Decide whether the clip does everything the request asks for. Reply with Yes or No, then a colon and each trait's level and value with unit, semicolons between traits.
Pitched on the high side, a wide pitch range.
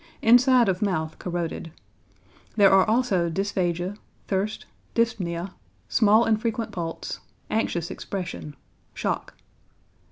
No: high, 195 Hz; average, 4.4 semitones